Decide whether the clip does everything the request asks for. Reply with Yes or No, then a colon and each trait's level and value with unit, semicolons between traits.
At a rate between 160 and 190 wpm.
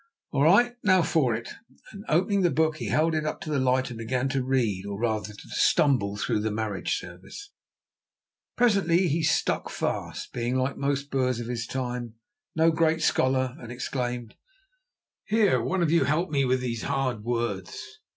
Yes: average, 180 wpm